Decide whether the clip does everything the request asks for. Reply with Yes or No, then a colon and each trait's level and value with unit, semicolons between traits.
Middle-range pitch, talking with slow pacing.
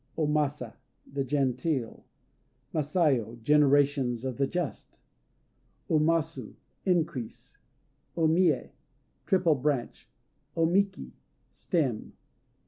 Yes: medium, 145 Hz; slow, 90 wpm